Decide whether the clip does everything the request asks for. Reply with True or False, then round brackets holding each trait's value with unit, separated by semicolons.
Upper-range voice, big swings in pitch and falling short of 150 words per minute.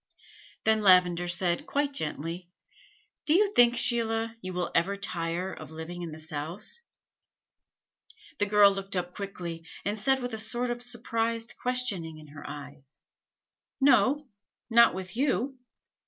True (200 Hz; 5.7 semitones; 140 wpm)